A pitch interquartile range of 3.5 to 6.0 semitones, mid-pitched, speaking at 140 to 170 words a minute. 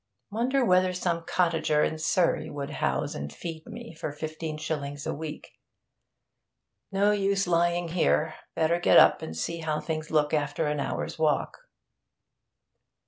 No: average, 2.8 semitones; medium, 160 Hz; average, 145 wpm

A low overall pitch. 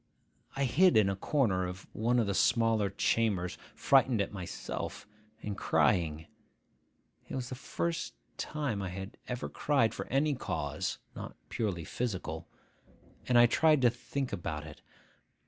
Yes: low, 110 Hz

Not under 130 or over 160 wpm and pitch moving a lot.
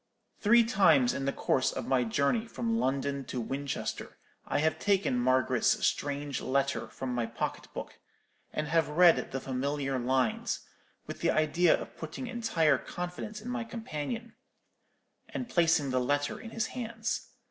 Yes: average, 155 wpm; wide, 8.2 semitones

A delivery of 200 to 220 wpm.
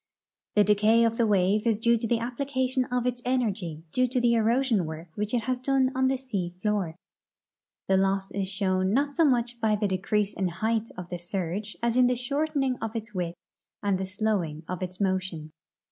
Yes: fast, 205 wpm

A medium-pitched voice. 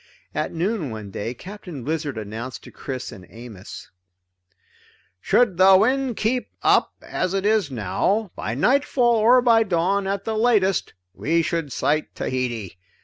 Yes: medium, 175 Hz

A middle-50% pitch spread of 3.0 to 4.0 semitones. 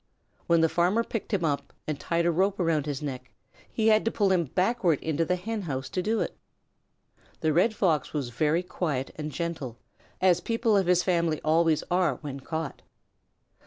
Yes: average, 3.7 semitones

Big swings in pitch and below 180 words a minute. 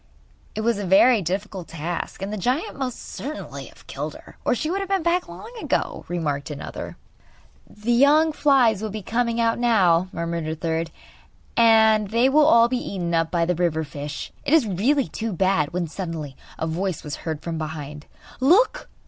No: wide, 6.7 semitones; average, 190 wpm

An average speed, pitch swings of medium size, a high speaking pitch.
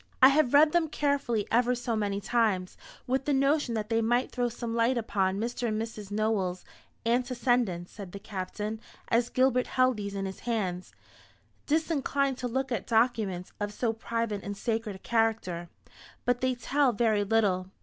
Yes: average, 170 wpm; average, 3.5 semitones; high, 230 Hz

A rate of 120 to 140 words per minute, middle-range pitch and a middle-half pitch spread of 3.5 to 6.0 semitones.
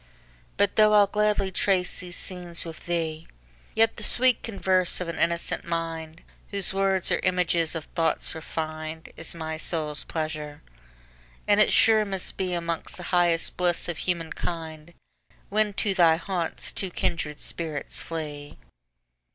No: slow, 135 wpm; medium, 170 Hz; average, 3.0 semitones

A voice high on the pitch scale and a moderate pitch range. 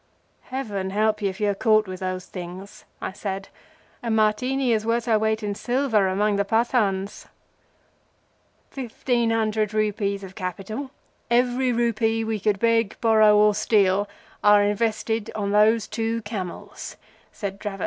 No: high, 215 Hz; narrow, 2.2 semitones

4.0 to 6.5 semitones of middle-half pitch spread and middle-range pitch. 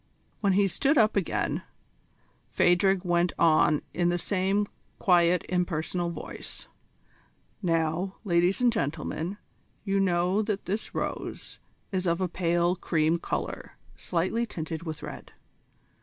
No: narrow, 2.5 semitones; medium, 180 Hz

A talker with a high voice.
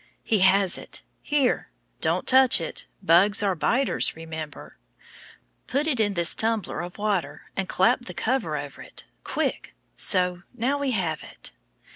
Yes: high, 195 Hz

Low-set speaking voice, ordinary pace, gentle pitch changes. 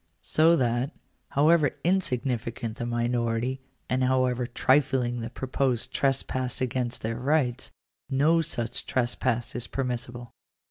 No: low, 125 Hz; slow, 110 wpm; narrow, 2.1 semitones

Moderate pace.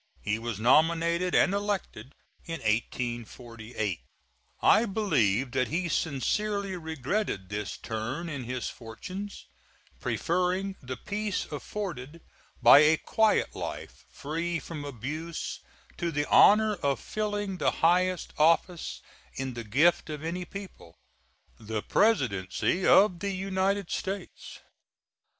No: slow, 115 wpm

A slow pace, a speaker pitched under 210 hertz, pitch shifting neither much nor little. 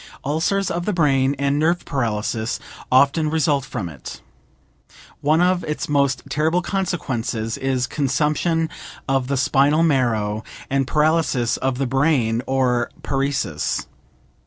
Yes: slow, 125 wpm; medium, 140 Hz; average, 3.6 semitones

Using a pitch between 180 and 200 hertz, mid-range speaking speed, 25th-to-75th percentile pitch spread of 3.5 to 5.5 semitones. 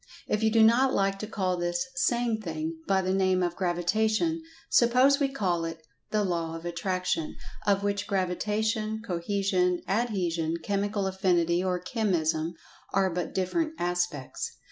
Yes: high, 190 Hz; average, 145 wpm; average, 3.8 semitones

